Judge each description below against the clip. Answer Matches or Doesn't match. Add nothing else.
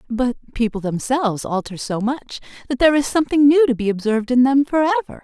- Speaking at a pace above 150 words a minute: Matches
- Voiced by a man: Doesn't match